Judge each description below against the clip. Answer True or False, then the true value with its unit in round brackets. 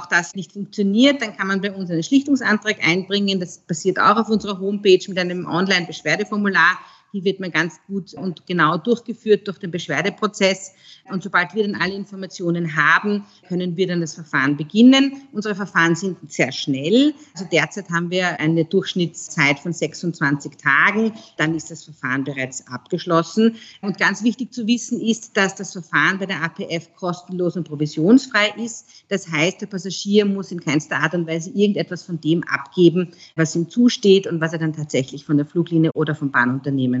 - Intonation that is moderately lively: True (3.8 semitones)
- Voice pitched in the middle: True (180 Hz)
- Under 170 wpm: False (175 wpm)